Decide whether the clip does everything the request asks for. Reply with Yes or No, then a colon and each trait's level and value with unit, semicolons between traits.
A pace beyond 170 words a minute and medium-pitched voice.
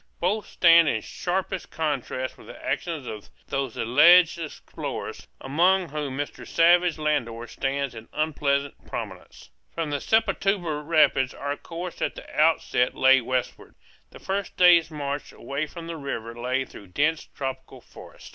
No: average, 145 wpm; medium, 150 Hz